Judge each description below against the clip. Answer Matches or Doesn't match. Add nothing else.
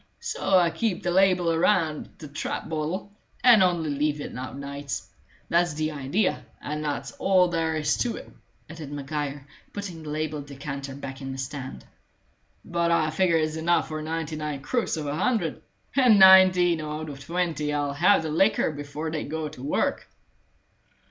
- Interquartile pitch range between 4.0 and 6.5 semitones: Doesn't match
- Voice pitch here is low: Doesn't match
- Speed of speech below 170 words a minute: Doesn't match